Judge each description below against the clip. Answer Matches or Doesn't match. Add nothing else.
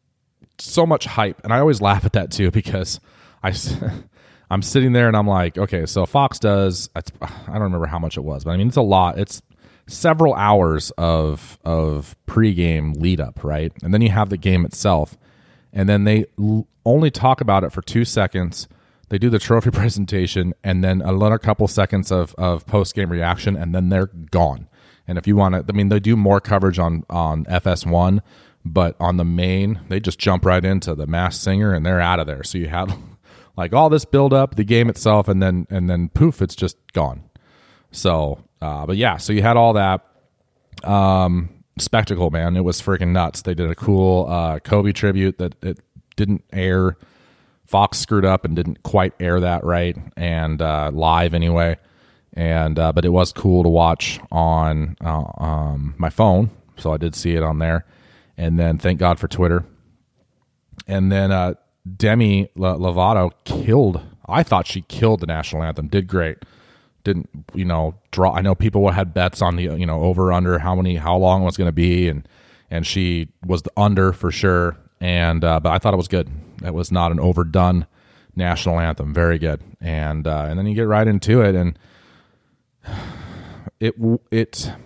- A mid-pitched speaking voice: Doesn't match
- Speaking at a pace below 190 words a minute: Doesn't match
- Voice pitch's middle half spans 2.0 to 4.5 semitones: Matches